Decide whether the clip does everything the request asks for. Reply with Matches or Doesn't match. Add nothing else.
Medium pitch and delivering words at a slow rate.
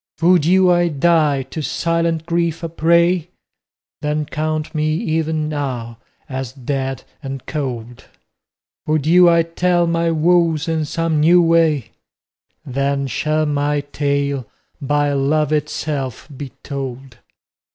Matches